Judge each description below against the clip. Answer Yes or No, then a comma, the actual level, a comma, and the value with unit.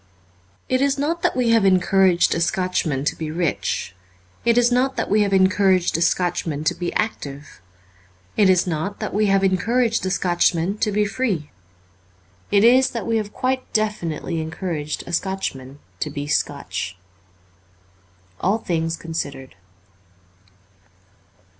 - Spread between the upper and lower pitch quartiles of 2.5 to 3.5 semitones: No, average, 5.0 semitones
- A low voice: No, high, 190 Hz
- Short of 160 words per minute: Yes, average, 145 wpm